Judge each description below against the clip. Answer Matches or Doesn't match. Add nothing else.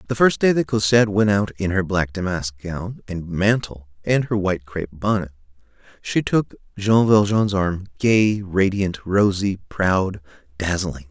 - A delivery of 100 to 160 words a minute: Matches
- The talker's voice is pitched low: Matches